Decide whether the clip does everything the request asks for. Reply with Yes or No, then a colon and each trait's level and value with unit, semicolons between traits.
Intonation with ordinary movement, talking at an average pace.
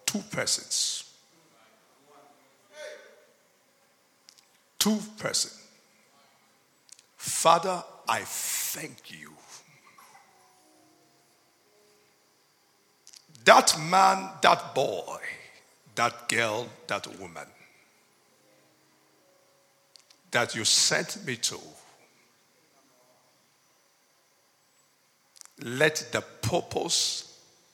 No: average, 4.2 semitones; slow, 50 wpm